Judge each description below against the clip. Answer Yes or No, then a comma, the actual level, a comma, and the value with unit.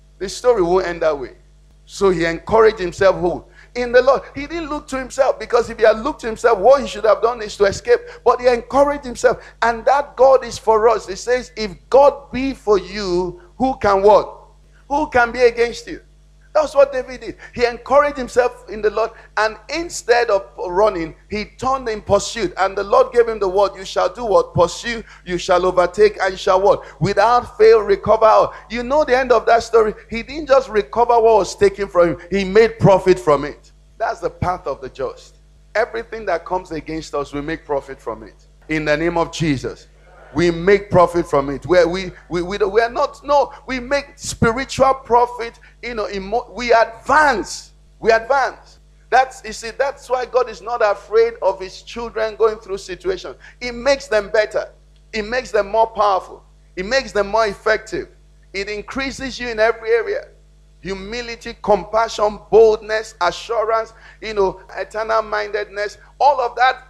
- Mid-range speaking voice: No, high, 225 Hz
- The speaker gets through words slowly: No, average, 190 wpm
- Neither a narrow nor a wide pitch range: Yes, average, 4.7 semitones